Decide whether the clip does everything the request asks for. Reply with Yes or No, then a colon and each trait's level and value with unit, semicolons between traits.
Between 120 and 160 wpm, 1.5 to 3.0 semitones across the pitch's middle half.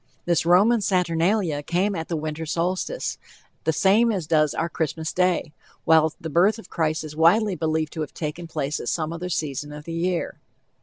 No: average, 190 wpm; average, 2.7 semitones